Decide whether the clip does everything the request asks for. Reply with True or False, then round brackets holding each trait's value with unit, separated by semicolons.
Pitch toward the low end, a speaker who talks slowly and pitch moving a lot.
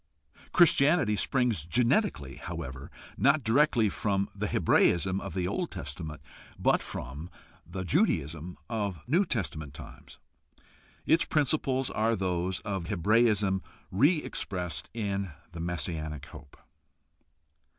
True (100 Hz; 110 wpm; 6.6 semitones)